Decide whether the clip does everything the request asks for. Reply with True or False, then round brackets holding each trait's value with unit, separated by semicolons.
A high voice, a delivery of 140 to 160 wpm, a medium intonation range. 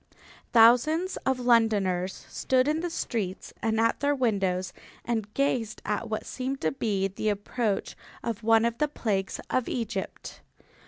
True (225 Hz; 150 wpm; 3.9 semitones)